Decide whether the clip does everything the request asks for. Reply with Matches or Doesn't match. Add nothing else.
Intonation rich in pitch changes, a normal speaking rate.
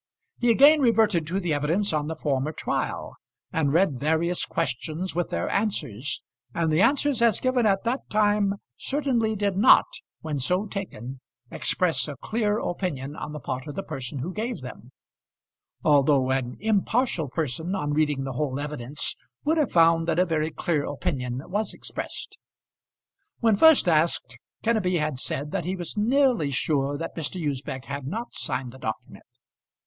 Matches